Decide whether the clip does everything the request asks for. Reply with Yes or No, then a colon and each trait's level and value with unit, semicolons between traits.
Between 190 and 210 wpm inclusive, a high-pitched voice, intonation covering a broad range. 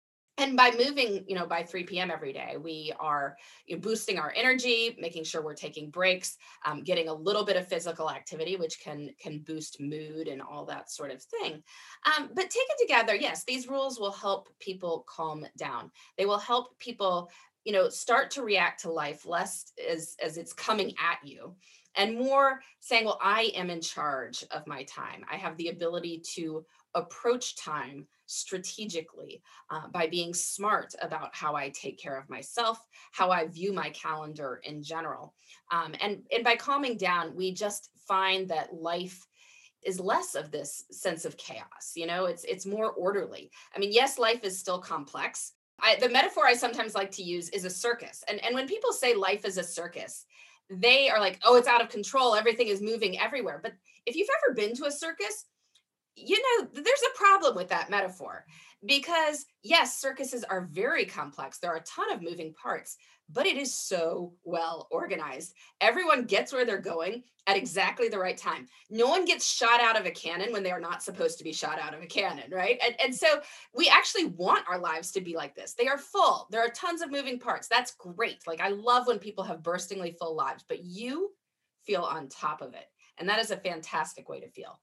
Yes: average, 200 wpm; high, 205 Hz; wide, 7.0 semitones